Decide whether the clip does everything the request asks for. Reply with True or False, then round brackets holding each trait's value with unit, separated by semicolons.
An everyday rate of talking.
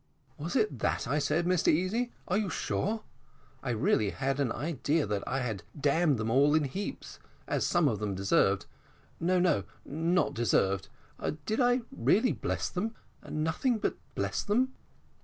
True (160 wpm)